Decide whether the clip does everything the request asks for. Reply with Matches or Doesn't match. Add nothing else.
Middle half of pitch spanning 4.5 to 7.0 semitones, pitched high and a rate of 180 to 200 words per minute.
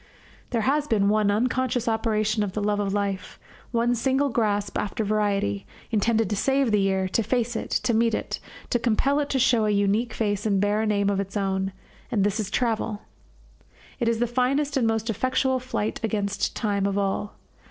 Doesn't match